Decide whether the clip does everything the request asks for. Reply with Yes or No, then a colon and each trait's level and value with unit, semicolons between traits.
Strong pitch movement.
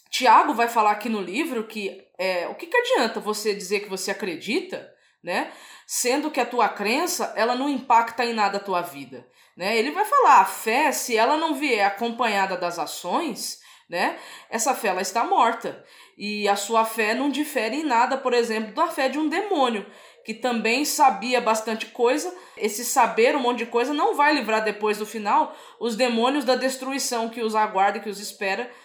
No: average, 4.2 semitones